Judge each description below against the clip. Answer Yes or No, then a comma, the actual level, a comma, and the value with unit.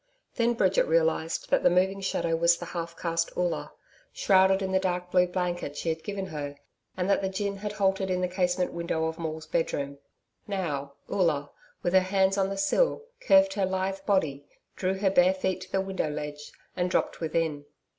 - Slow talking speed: No, average, 195 wpm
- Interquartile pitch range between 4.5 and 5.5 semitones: No, average, 2.7 semitones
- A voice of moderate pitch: Yes, medium, 180 Hz